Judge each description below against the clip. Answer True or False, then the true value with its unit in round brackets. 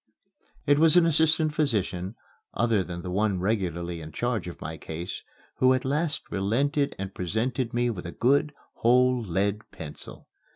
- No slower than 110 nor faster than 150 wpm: False (160 wpm)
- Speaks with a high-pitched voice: False (110 Hz)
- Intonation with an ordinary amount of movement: False (7.0 semitones)